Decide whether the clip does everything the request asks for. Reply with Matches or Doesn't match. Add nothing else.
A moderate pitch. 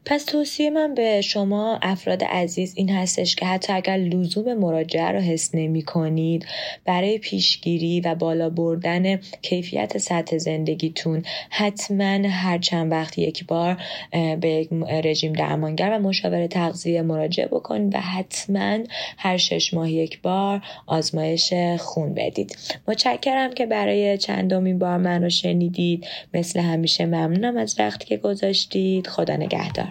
Matches